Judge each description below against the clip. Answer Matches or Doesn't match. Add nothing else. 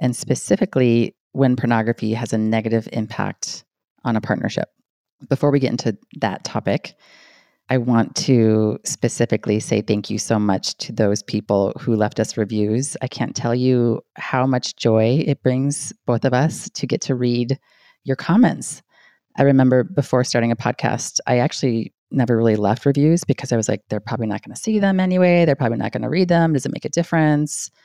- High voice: Doesn't match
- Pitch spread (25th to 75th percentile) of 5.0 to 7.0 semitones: Doesn't match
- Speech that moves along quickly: Doesn't match